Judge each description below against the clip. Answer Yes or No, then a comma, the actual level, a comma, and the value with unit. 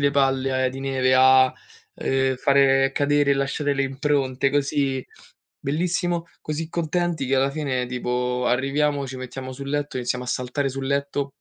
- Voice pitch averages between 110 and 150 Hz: Yes, low, 135 Hz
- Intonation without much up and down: Yes, narrow, 1.7 semitones